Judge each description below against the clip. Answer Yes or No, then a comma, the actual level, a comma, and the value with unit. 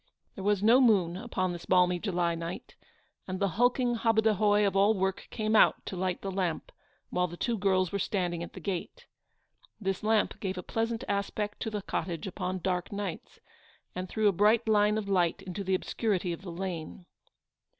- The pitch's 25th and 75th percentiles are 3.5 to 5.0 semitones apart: No, average, 2.9 semitones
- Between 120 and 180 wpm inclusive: No, average, 190 wpm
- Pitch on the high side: Yes, high, 195 Hz